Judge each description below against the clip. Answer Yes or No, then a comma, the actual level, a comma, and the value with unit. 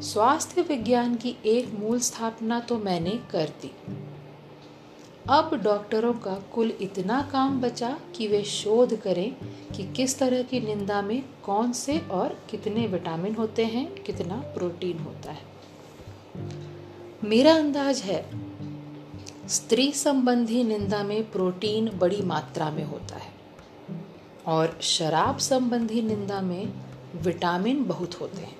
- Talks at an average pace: Yes, average, 125 wpm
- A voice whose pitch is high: Yes, high, 210 Hz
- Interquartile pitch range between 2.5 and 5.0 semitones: No, wide, 5.6 semitones